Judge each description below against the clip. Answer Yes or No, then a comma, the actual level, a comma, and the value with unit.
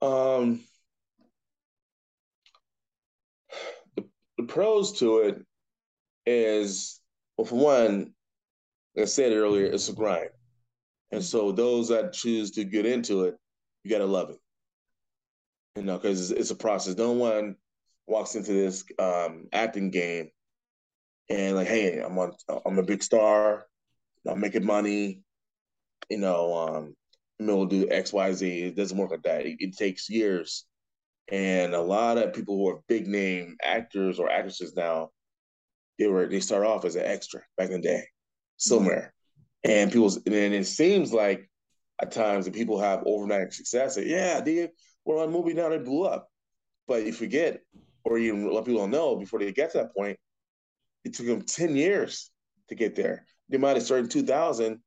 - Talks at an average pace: Yes, average, 165 wpm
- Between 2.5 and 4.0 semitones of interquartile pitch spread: Yes, average, 3.5 semitones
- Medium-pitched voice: No, low, 105 Hz